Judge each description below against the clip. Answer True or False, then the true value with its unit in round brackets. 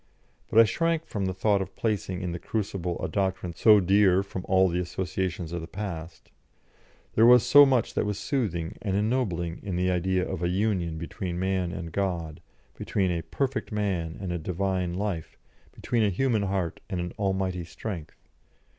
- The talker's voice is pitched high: False (95 Hz)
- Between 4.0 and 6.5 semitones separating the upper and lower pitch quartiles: False (3.0 semitones)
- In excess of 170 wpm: True (180 wpm)